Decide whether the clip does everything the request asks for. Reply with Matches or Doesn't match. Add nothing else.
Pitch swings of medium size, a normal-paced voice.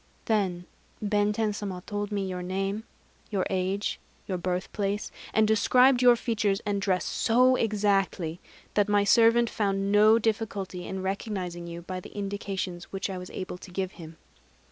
Doesn't match